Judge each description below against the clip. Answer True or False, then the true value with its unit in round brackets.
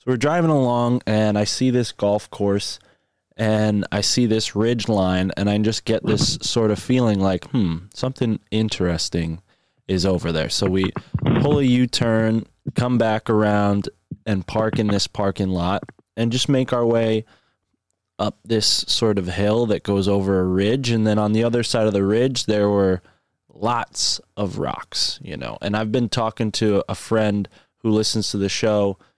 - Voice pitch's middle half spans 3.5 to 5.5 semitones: False (2.9 semitones)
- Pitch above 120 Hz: False (110 Hz)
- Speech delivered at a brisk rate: False (185 wpm)